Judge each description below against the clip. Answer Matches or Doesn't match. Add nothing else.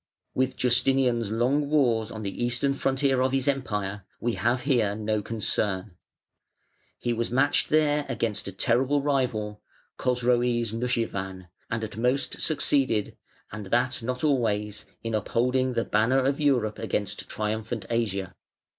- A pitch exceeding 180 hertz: Doesn't match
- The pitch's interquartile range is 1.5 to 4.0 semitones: Matches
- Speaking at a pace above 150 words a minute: Doesn't match